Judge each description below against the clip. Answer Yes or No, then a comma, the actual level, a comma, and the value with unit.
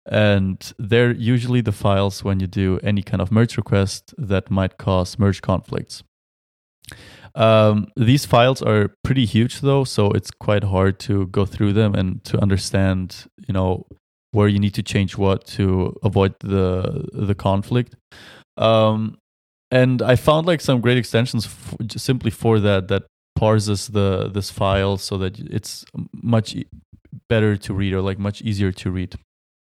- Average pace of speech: Yes, average, 160 wpm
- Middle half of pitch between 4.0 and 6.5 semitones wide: No, average, 3.0 semitones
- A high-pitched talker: No, low, 105 Hz